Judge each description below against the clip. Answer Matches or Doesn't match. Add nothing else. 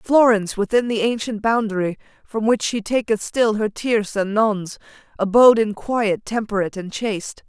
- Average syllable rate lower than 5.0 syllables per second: Doesn't match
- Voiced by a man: Doesn't match